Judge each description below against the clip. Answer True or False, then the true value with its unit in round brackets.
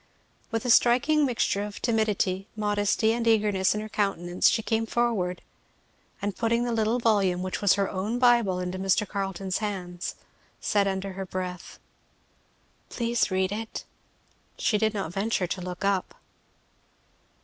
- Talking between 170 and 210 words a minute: False (150 wpm)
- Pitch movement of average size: True (3.2 semitones)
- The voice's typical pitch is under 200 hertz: False (205 Hz)